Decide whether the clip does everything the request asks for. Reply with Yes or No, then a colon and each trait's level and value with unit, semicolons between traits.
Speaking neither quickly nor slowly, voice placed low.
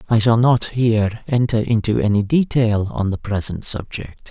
Yes: average, 165 wpm; low, 110 Hz